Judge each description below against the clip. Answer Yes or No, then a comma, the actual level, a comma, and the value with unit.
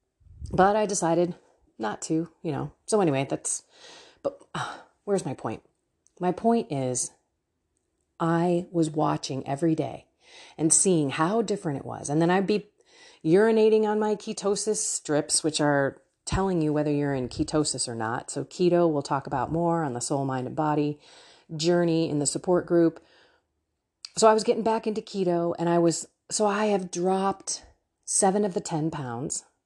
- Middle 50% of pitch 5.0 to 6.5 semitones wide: Yes, average, 5.3 semitones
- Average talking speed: Yes, average, 170 wpm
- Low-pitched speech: No, medium, 170 Hz